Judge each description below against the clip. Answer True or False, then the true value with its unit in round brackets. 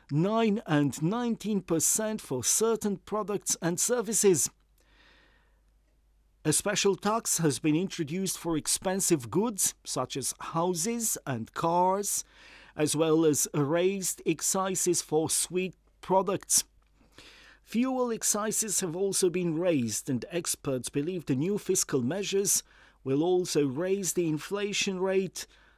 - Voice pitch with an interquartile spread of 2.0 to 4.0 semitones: False (4.5 semitones)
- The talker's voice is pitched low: False (180 Hz)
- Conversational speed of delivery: False (115 wpm)